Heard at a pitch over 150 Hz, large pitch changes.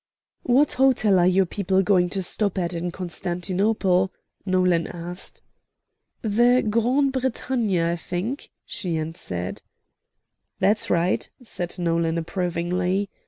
No: medium, 185 Hz; average, 3.6 semitones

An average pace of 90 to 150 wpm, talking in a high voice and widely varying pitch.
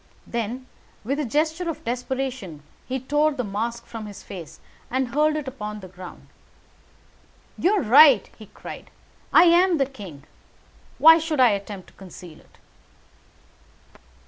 Yes: average, 145 wpm; very high, 255 Hz; wide, 6.5 semitones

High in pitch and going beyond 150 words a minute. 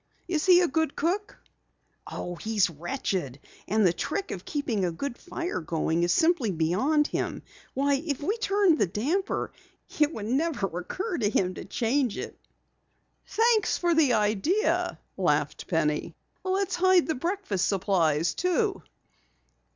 No: very high, 285 Hz; average, 145 wpm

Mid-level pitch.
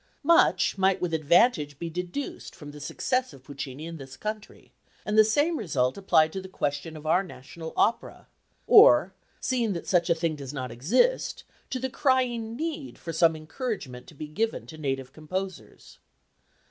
Yes: medium, 170 Hz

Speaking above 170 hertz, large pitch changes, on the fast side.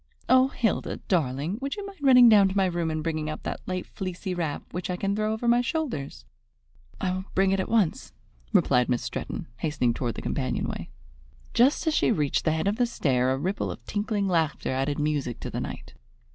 Yes: medium, 185 Hz; wide, 6.6 semitones; fast, 215 wpm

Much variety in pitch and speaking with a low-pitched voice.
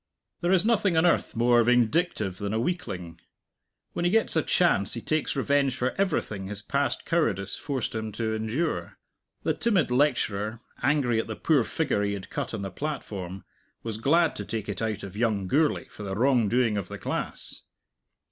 Yes: wide, 6.7 semitones; low, 120 Hz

